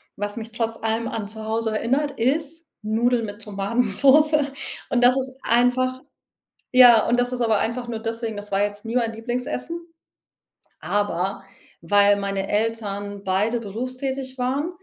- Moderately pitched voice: No, high, 230 Hz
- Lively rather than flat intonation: No, average, 3.5 semitones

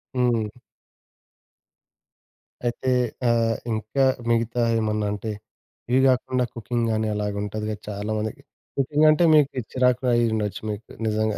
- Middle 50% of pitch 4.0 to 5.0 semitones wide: No, average, 2.8 semitones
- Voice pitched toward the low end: Yes, low, 115 Hz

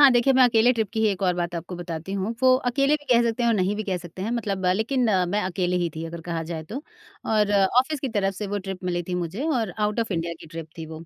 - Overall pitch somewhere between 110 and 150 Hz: No, high, 195 Hz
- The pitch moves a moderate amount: Yes, average, 5.0 semitones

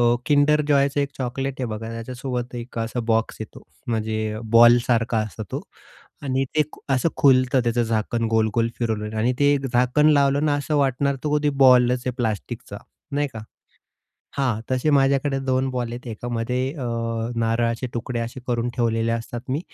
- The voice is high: No, low, 125 Hz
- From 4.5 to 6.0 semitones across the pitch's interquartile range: No, average, 2.8 semitones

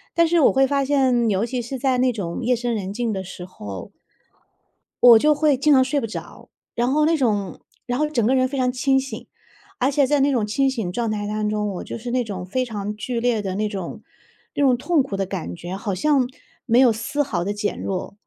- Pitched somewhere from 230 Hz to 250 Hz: Yes, high, 240 Hz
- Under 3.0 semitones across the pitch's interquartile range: No, average, 4.4 semitones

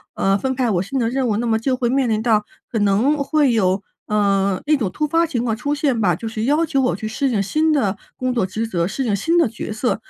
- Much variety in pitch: No, average, 4.7 semitones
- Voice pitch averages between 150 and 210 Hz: No, high, 235 Hz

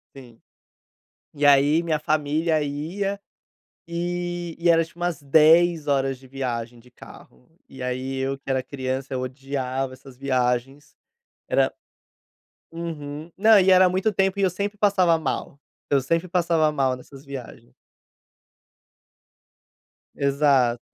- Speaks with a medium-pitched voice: Yes, medium, 145 Hz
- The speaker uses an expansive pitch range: No, average, 4.2 semitones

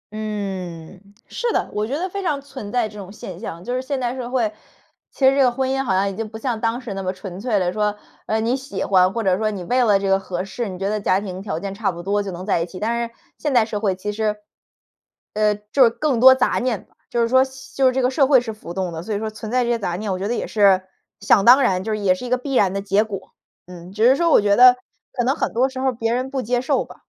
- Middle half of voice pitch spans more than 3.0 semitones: Yes, average, 4.3 semitones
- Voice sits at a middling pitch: No, high, 215 Hz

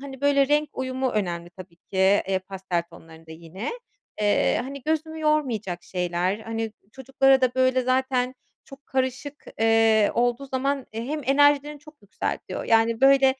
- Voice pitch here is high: Yes, very high, 255 Hz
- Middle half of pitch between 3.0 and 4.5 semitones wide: No, average, 5.2 semitones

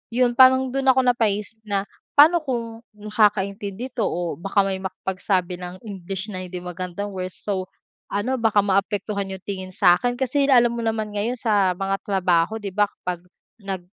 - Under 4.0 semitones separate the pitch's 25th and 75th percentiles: Yes, average, 3.6 semitones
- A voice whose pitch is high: Yes, high, 205 Hz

